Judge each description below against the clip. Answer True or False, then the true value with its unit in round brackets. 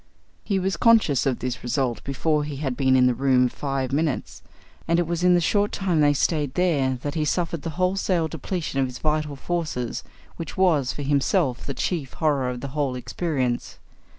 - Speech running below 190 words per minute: False (195 wpm)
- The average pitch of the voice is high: False (145 Hz)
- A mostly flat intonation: False (4.3 semitones)